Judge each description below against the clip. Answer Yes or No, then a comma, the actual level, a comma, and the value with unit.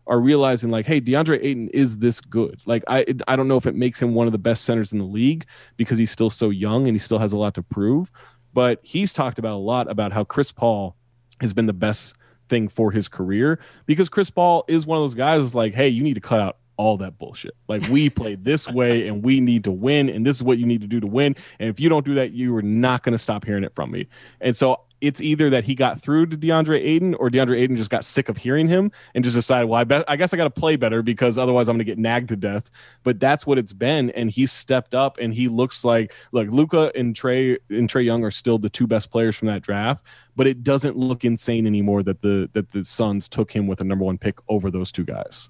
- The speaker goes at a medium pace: No, fast, 270 wpm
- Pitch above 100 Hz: Yes, low, 120 Hz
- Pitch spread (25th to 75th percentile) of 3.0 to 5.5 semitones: Yes, average, 3.4 semitones